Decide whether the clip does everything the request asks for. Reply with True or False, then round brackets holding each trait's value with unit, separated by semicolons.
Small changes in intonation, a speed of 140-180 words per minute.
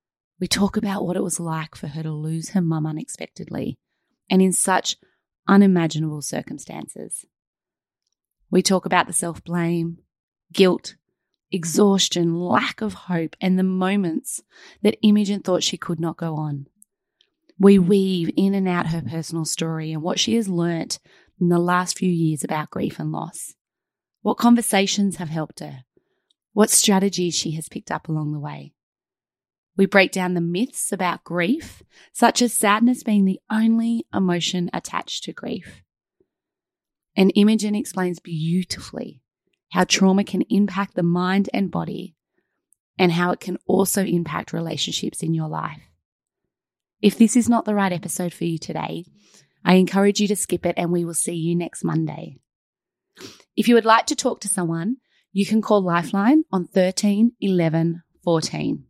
False (3.1 semitones; 160 wpm)